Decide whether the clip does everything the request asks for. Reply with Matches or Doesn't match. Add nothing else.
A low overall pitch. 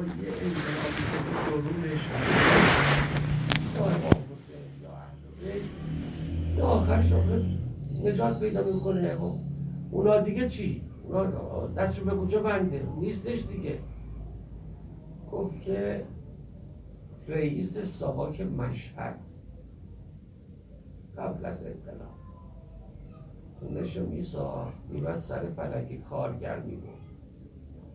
Matches